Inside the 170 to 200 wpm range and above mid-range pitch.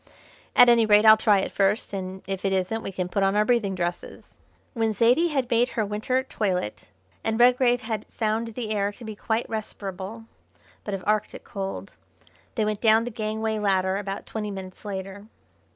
Yes: average, 185 wpm; high, 215 Hz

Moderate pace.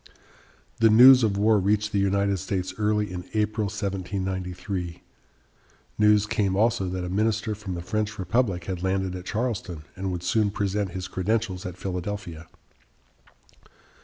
Yes: average, 145 wpm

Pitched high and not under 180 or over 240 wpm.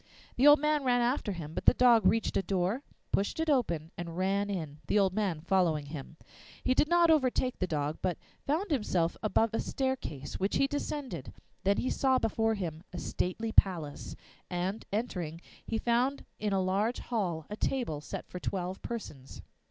Yes: high, 200 Hz; average, 185 wpm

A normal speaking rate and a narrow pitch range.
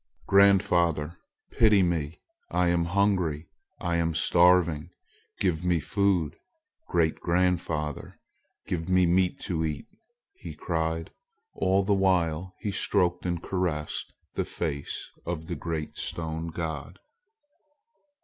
No: slow, 115 wpm; narrow, 2.3 semitones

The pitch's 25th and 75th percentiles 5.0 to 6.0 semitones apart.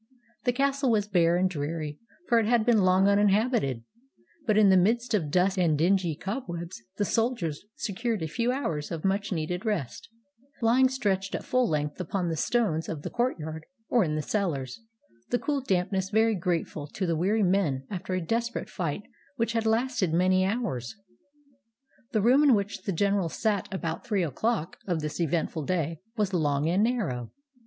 Yes: wide, 5.5 semitones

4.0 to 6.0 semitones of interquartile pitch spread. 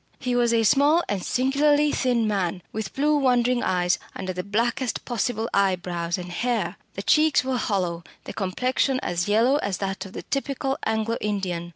Yes: wide, 5.6 semitones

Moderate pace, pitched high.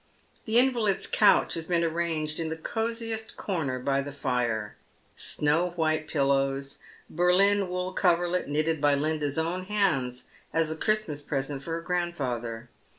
No: average, 150 wpm; medium, 160 Hz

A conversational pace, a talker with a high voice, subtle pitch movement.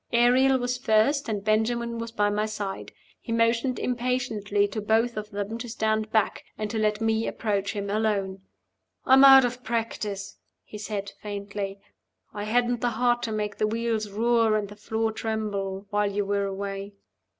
Yes: average, 175 wpm; high, 215 Hz; narrow, 2.2 semitones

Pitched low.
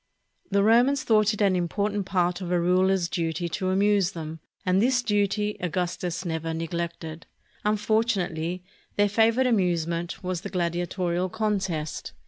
No: medium, 185 Hz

